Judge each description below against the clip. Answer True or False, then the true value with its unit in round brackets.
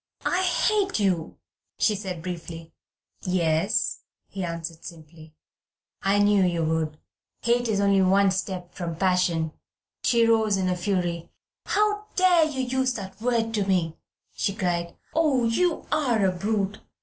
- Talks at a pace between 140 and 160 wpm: True (145 wpm)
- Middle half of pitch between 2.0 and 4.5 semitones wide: False (5.0 semitones)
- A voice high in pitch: True (195 Hz)